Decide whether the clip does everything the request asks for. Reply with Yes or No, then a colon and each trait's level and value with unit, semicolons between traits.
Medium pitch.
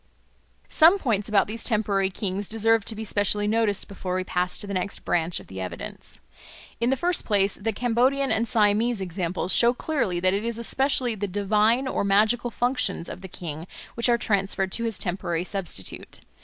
No: high, 210 Hz